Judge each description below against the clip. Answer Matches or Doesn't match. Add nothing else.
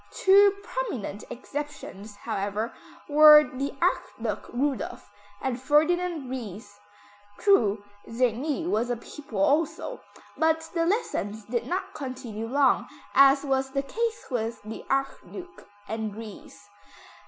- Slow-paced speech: Matches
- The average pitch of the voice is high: Matches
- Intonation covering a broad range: Matches